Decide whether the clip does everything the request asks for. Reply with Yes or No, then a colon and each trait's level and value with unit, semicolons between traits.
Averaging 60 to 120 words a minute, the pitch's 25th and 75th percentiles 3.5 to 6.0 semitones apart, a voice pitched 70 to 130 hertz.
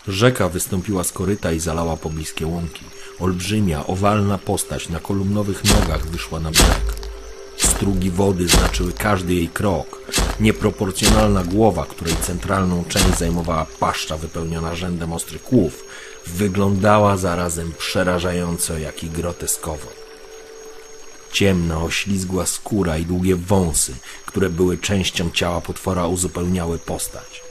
No: average, 115 wpm; average, 3.1 semitones; very low, 90 Hz